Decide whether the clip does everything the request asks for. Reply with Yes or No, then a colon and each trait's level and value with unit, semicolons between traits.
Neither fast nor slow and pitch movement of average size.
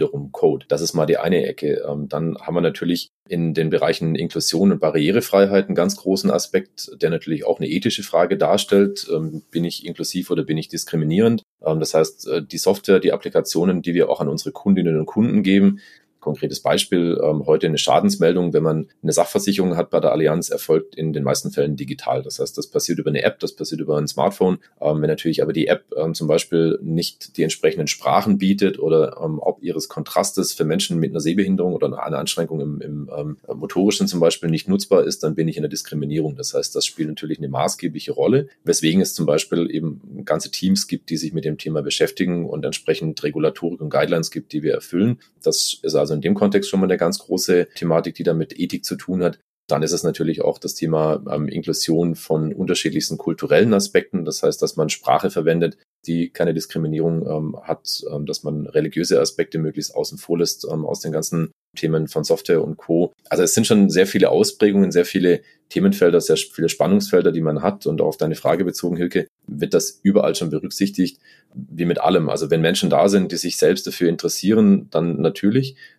No: fast, 205 wpm; average, 3.9 semitones